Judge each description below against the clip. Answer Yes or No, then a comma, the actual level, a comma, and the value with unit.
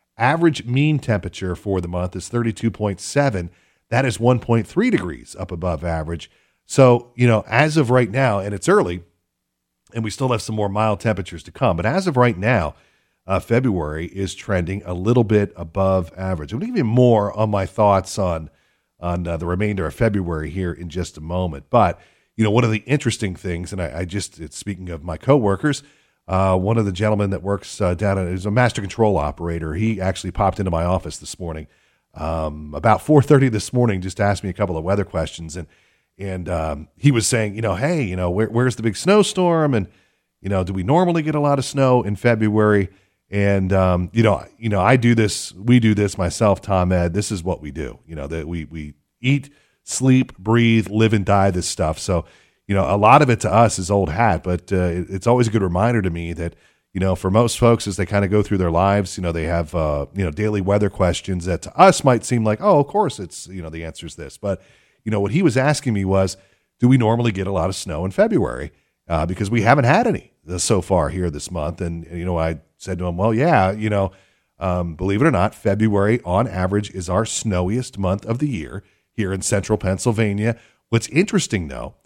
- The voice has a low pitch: Yes, low, 100 Hz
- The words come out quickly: Yes, fast, 225 wpm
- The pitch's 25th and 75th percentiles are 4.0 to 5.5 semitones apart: Yes, average, 4.4 semitones